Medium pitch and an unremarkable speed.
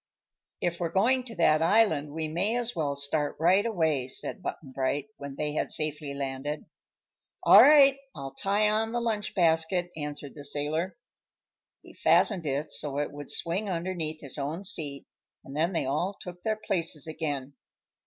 Yes: medium, 160 Hz; average, 170 wpm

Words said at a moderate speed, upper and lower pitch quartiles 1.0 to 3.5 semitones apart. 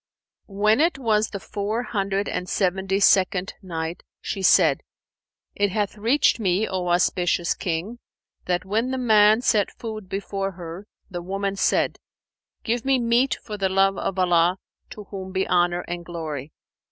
Yes: average, 155 wpm; average, 3.1 semitones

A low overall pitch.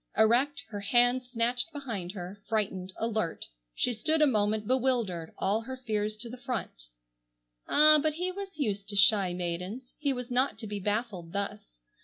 No: high, 225 Hz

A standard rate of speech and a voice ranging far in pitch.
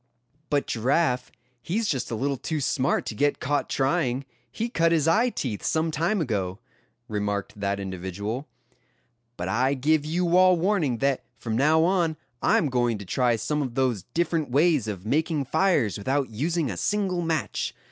Yes: average, 170 wpm; wide, 6.2 semitones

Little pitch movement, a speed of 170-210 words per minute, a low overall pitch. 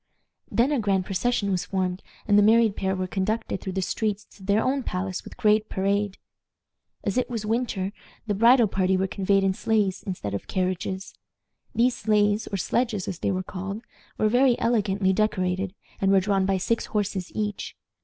No: narrow, 2.3 semitones; average, 185 wpm; high, 200 Hz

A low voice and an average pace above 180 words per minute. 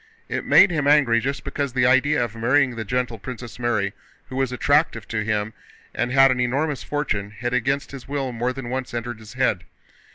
Yes: low, 125 Hz; average, 200 wpm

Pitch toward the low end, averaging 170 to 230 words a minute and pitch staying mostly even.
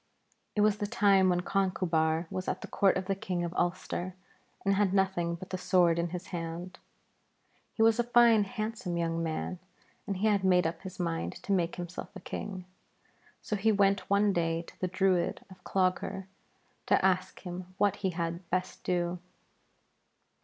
No: medium, 185 Hz; average, 180 wpm; narrow, 2.2 semitones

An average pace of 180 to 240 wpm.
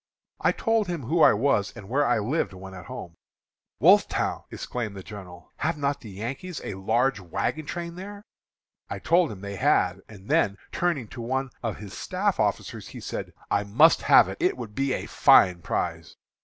Yes: average, 190 wpm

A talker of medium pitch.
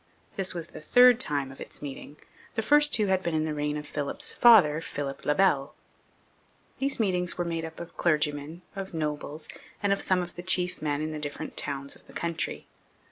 Yes: medium, 165 Hz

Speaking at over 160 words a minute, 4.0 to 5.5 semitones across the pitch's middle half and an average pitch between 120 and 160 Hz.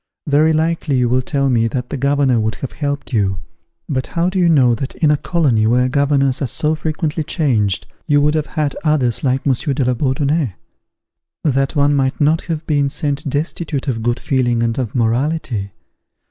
No: average, 190 wpm; average, 3.4 semitones; medium, 140 Hz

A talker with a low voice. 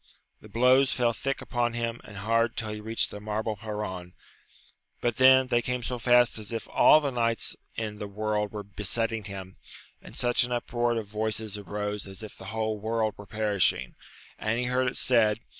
Yes: low, 110 Hz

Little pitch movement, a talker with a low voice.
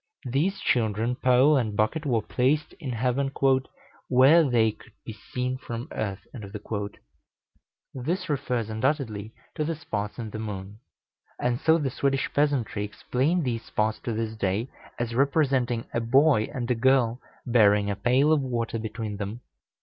No: average, 3.8 semitones; low, 120 Hz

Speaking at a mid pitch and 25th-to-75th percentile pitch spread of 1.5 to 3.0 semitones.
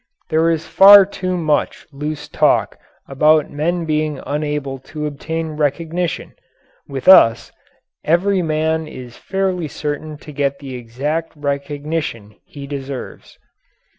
Yes: medium, 150 Hz; narrow, 2.6 semitones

